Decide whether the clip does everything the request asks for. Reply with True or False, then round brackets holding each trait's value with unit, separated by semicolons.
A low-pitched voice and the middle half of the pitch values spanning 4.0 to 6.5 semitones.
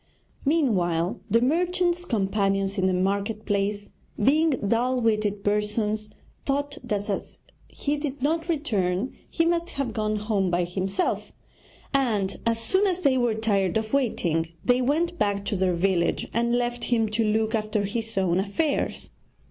False (220 Hz; 5.4 semitones)